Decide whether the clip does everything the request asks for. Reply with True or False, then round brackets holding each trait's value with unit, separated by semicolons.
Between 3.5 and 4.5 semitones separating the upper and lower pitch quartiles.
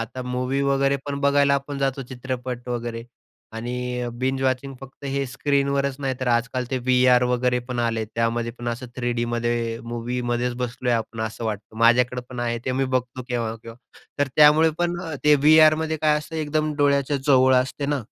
False (2.7 semitones)